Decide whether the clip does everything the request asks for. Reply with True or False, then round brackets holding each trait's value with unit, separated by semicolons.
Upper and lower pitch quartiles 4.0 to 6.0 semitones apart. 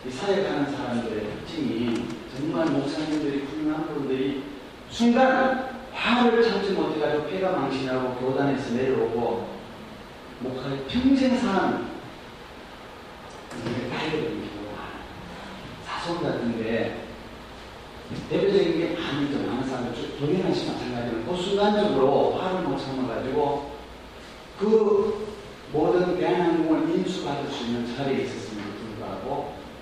False (8.5 semitones)